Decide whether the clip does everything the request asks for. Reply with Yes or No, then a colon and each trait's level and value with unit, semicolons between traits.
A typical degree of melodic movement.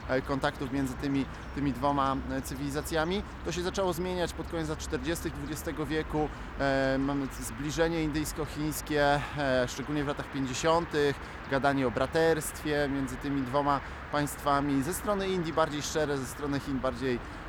No: narrow, 2.2 semitones